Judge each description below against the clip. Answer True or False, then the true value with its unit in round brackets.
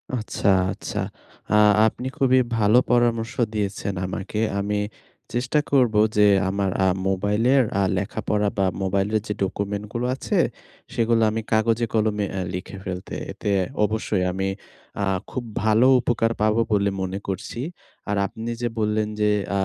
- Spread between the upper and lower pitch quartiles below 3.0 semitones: True (2.4 semitones)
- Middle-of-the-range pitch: False (105 Hz)